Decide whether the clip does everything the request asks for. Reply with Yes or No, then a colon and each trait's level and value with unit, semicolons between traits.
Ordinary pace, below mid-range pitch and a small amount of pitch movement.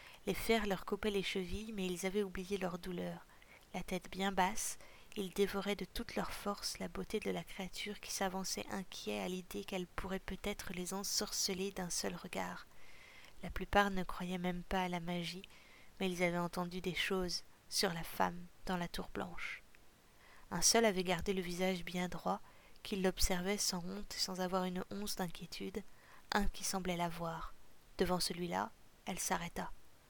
No: average, 175 wpm; medium, 185 Hz; narrow, 1.7 semitones